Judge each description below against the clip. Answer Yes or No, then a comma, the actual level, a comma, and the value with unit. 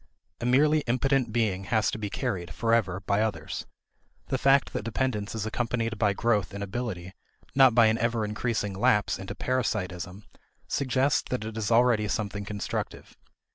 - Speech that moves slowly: No, average, 160 wpm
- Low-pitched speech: Yes, low, 110 Hz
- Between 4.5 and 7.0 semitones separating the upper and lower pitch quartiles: No, average, 3.2 semitones